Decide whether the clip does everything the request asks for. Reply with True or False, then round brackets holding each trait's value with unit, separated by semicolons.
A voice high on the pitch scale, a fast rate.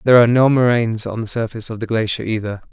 False (115 Hz; 245 wpm)